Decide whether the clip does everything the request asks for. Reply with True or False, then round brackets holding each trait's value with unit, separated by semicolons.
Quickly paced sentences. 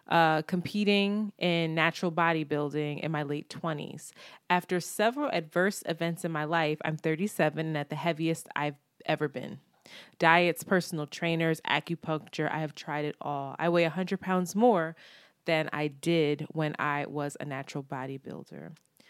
False (150 wpm)